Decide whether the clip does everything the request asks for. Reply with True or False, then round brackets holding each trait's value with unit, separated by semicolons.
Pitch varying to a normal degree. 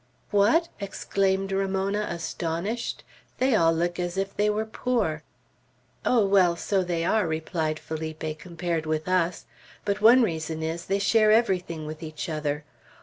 True (4.2 semitones)